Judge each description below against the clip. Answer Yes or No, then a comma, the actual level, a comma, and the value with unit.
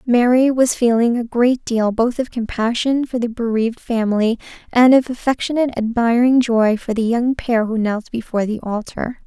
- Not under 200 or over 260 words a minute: No, average, 175 wpm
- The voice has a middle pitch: No, high, 235 Hz